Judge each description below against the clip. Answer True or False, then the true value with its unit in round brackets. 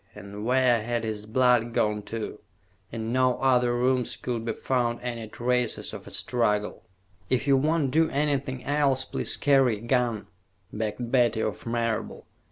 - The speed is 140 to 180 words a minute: True (160 wpm)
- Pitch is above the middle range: False (120 Hz)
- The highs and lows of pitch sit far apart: False (2.5 semitones)